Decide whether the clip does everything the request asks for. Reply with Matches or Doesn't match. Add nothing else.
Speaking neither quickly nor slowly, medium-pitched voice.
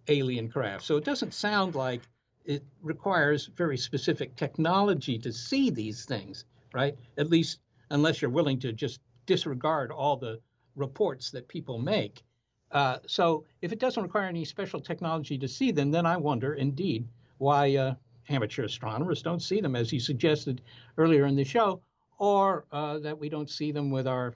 Matches